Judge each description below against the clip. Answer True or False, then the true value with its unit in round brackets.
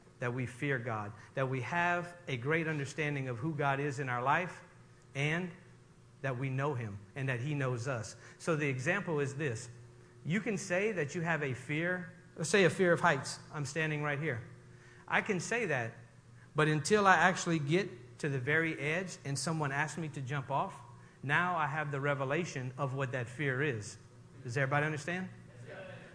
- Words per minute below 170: False (190 wpm)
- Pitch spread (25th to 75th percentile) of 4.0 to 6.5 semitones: True (4.4 semitones)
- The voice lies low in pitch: False (145 Hz)